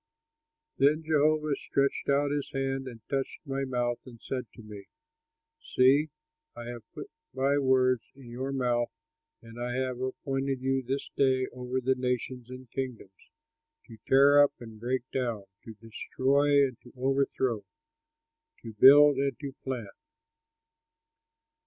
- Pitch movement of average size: No, narrow, 2.2 semitones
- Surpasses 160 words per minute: No, average, 140 wpm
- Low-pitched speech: Yes, low, 130 Hz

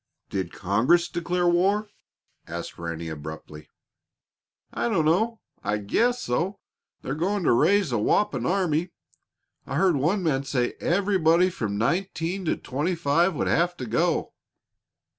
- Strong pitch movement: Yes, wide, 7.3 semitones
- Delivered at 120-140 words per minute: Yes, slow, 135 wpm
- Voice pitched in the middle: Yes, medium, 165 Hz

